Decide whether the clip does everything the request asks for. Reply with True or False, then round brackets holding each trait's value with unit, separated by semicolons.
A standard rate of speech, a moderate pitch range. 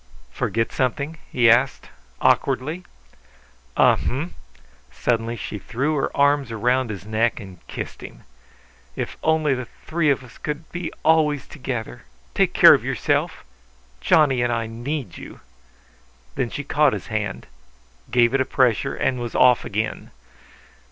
True (145 wpm; 4.1 semitones)